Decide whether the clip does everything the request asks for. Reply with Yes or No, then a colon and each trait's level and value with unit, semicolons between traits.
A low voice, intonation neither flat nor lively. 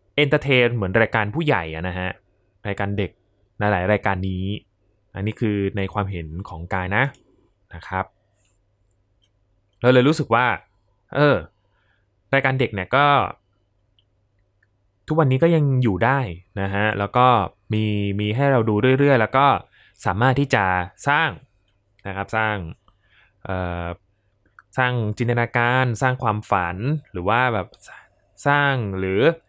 Yes: low, 105 Hz; average, 4.0 semitones